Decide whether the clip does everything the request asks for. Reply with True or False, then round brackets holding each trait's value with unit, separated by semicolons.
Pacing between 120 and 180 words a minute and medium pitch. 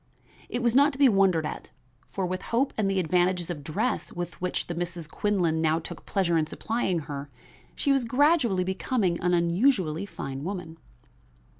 True (175 wpm; 180 Hz)